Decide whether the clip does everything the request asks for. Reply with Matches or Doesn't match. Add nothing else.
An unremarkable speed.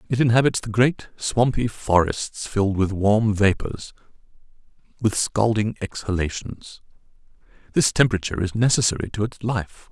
Doesn't match